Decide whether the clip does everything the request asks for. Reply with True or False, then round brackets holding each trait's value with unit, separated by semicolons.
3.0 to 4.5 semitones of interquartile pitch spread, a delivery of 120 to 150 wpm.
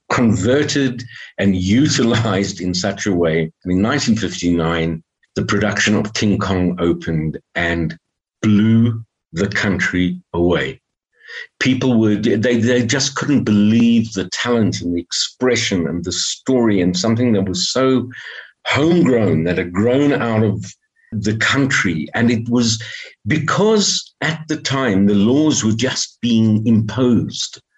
False (5.1 semitones; 135 wpm)